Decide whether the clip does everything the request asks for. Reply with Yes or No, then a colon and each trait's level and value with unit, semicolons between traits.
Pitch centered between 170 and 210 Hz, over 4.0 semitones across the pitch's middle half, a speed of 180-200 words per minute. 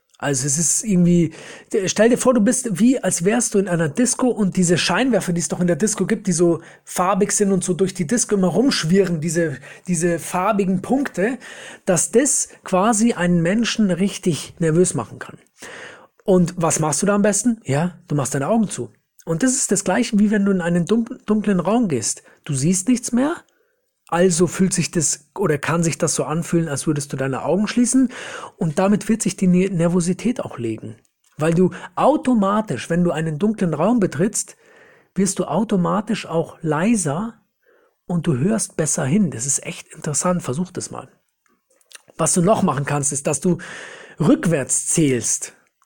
Yes: medium, 185 Hz; average, 4.7 semitones; average, 185 wpm